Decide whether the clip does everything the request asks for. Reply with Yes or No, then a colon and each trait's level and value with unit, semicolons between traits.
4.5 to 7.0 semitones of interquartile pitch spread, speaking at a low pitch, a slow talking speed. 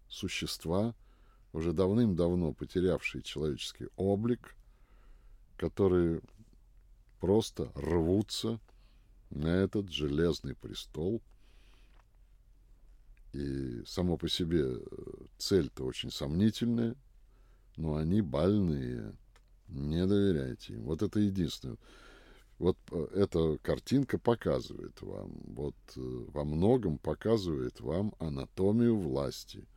Yes: average, 5.1 semitones; very low, 95 Hz; slow, 85 wpm